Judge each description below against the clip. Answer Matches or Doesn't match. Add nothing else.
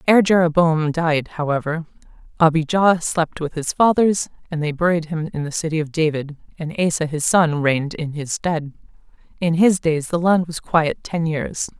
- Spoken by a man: Doesn't match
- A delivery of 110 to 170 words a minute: Doesn't match